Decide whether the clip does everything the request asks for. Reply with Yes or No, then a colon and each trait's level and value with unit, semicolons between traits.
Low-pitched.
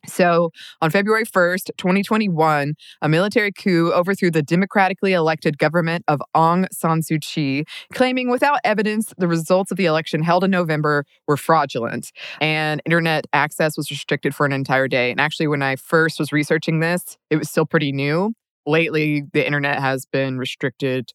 No: medium, 160 Hz